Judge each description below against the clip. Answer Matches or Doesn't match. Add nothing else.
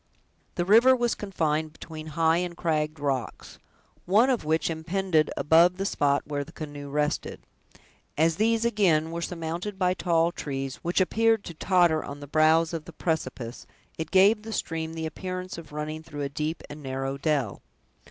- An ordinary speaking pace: Matches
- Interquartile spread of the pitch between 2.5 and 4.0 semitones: Matches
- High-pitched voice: Doesn't match